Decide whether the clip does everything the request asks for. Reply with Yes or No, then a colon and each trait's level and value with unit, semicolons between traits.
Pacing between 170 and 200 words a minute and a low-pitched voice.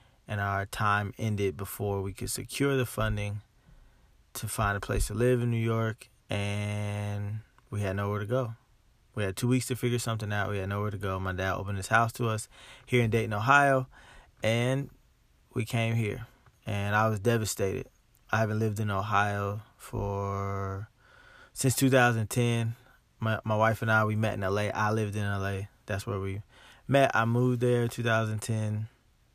Yes: average, 180 wpm; low, 110 Hz